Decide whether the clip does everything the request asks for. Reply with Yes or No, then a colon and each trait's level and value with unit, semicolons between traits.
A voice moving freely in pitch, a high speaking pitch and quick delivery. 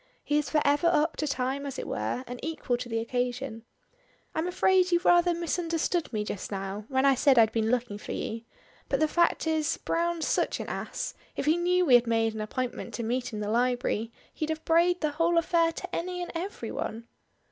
Yes: wide, 6.0 semitones; very high, 285 Hz; fast, 215 wpm